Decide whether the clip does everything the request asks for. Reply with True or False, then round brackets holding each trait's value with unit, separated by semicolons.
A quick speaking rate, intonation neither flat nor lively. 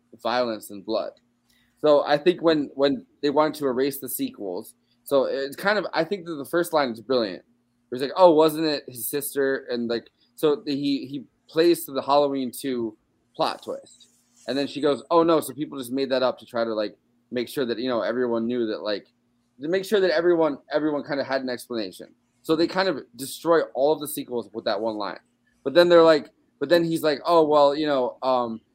True (230 wpm; 4.2 semitones)